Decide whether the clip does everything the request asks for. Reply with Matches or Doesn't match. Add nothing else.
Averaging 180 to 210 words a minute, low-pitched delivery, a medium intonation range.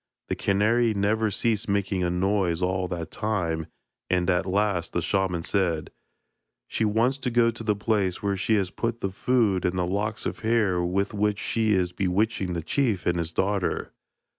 Matches